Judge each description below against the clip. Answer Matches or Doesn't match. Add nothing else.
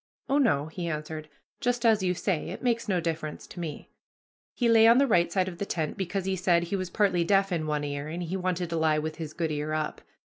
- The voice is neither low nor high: Matches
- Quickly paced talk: Matches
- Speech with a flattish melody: Doesn't match